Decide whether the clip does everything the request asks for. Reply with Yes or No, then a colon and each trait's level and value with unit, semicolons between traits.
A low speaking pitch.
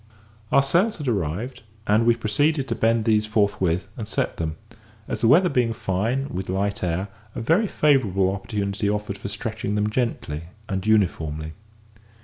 Yes: low, 105 Hz